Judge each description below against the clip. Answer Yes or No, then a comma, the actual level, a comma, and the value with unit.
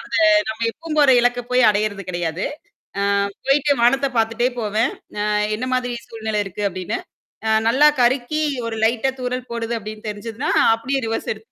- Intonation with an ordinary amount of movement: Yes, average, 3.0 semitones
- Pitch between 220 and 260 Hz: Yes, high, 230 Hz